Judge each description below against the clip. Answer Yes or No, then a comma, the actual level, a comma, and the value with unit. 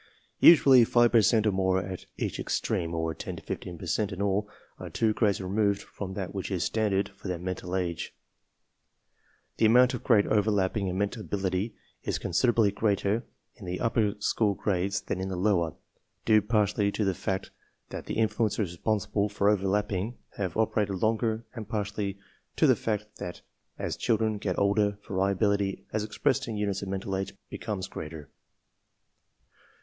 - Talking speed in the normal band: Yes, average, 175 wpm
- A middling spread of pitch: No, narrow, 2.2 semitones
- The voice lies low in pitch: Yes, low, 100 Hz